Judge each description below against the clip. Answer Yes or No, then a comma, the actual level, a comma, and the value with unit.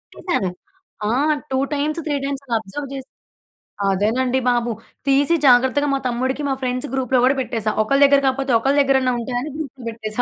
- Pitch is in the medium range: No, very high, 260 Hz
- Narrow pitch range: Yes, narrow, 2.3 semitones